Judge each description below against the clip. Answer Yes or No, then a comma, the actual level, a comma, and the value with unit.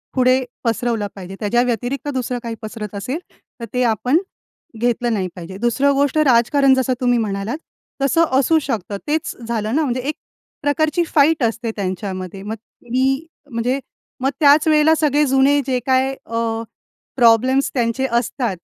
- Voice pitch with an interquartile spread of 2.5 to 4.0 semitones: Yes, average, 3.5 semitones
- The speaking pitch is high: Yes, very high, 250 Hz